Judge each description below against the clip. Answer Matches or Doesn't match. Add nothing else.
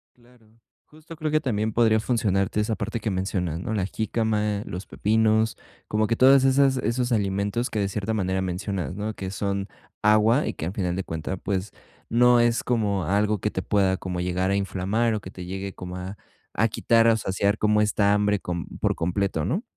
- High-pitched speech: Doesn't match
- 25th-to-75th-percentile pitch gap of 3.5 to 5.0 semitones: Doesn't match